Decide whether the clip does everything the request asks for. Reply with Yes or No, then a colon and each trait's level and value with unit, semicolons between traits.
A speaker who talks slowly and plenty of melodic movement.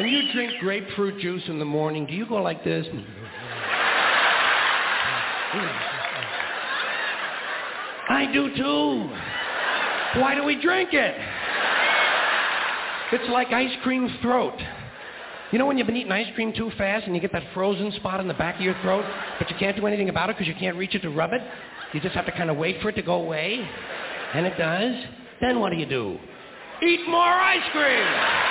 No: average, 185 wpm; wide, 5.7 semitones